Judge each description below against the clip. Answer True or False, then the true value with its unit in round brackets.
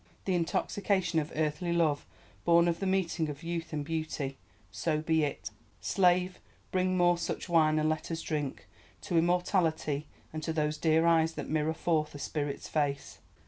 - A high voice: False (160 Hz)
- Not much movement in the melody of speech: True (2.1 semitones)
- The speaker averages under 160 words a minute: False (165 wpm)